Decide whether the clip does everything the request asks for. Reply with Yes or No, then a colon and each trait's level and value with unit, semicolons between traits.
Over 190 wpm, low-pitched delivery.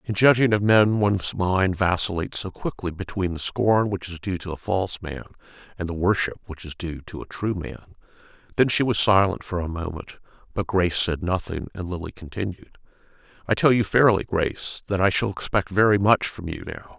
Yes: average, 200 wpm; very low, 95 Hz